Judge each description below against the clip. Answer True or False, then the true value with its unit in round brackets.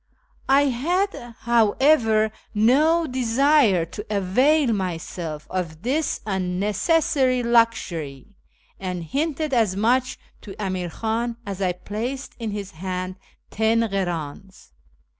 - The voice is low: False (220 Hz)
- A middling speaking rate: False (105 wpm)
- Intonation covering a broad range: True (5.7 semitones)